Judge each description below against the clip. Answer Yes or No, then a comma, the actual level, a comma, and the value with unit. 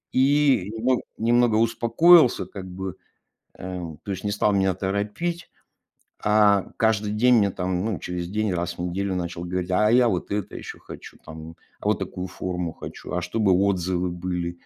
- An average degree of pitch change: Yes, average, 3.7 semitones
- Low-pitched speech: Yes, low, 100 Hz